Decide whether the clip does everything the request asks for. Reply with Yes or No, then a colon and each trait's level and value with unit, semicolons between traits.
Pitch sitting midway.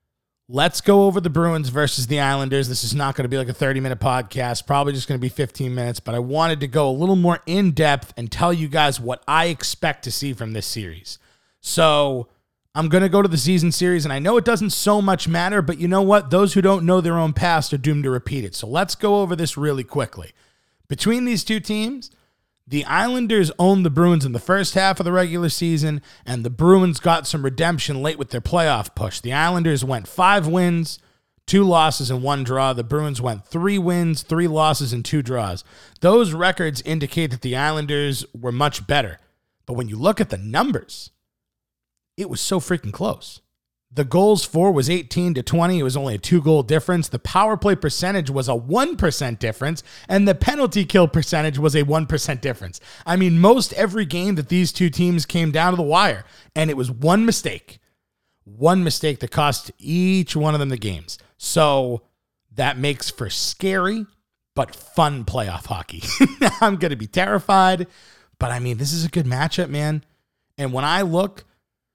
Yes: medium, 155 Hz